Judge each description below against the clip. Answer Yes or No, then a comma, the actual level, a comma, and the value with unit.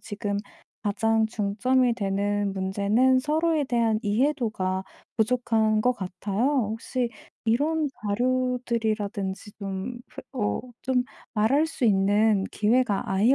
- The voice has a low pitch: No, high, 220 Hz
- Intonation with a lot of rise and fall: No, average, 3.7 semitones